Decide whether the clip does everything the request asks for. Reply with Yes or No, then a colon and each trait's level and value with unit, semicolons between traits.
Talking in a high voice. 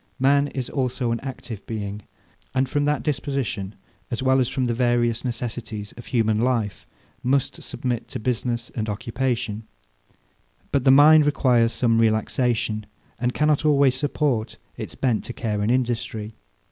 No: low, 120 Hz